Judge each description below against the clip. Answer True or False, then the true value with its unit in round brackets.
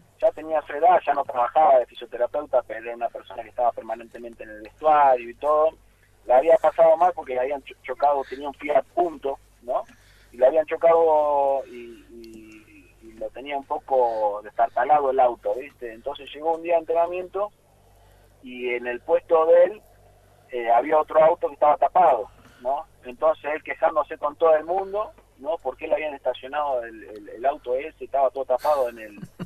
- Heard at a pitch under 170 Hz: True (140 Hz)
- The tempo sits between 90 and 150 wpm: False (185 wpm)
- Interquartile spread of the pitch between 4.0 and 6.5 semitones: True (5.3 semitones)